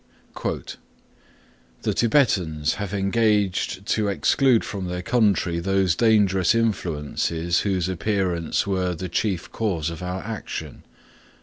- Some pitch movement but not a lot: Yes, average, 3.3 semitones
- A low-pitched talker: Yes, very low, 95 Hz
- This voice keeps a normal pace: No, slow, 115 wpm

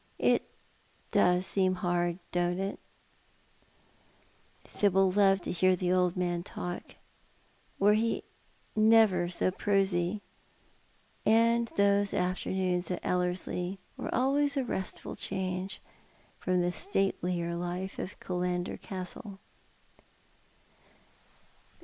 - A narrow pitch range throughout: Yes, narrow, 2.1 semitones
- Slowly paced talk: Yes, slow, 100 wpm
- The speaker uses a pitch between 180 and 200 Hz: Yes, medium, 185 Hz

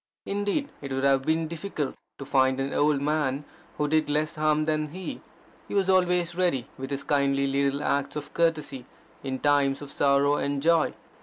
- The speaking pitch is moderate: Yes, medium, 145 Hz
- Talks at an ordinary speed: Yes, average, 180 wpm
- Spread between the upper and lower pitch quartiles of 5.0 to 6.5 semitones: No, narrow, 2.6 semitones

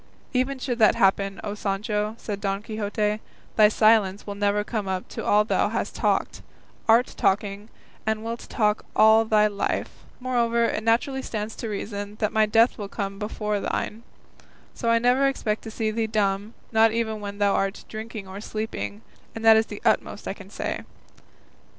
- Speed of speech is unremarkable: Yes, average, 180 wpm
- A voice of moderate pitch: No, high, 215 Hz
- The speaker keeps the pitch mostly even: Yes, narrow, 1.7 semitones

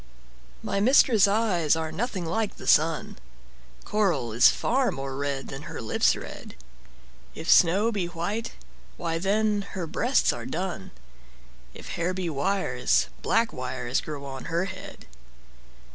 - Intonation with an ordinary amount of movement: No, wide, 5.9 semitones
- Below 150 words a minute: Yes, average, 140 wpm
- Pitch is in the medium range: Yes, medium, 175 Hz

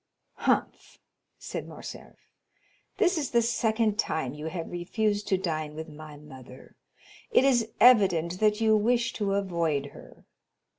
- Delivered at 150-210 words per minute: No, average, 140 wpm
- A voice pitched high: Yes, high, 195 Hz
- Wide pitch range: Yes, wide, 6.1 semitones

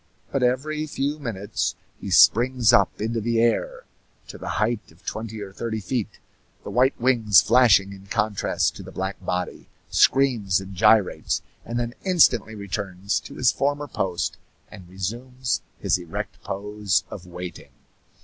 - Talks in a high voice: No, low, 110 Hz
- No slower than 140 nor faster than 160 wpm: Yes, average, 150 wpm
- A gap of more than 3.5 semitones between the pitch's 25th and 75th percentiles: Yes, average, 4.5 semitones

